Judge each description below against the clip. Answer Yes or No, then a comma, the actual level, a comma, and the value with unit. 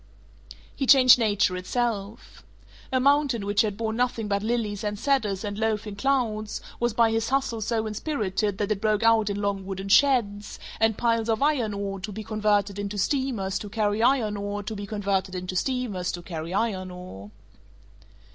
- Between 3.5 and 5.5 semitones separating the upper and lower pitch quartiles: No, narrow, 2.6 semitones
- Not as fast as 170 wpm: No, average, 175 wpm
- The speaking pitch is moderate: No, high, 210 Hz